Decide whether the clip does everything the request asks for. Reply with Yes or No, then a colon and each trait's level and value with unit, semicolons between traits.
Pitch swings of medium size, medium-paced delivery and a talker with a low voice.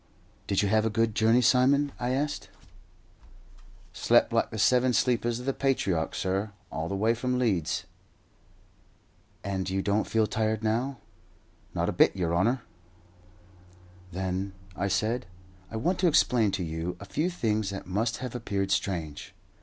Yes: average, 4.4 semitones; average, 155 wpm; low, 110 Hz